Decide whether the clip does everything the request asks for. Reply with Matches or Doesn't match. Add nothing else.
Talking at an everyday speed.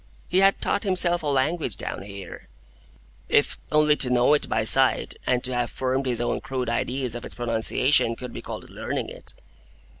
Matches